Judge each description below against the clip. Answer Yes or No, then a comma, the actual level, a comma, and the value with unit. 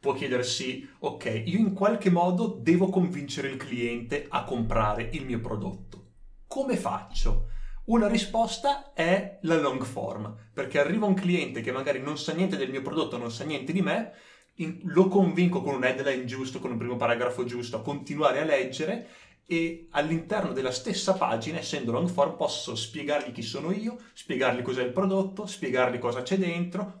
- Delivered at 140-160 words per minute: No, fast, 170 wpm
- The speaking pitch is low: No, medium, 145 Hz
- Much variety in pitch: Yes, wide, 7.3 semitones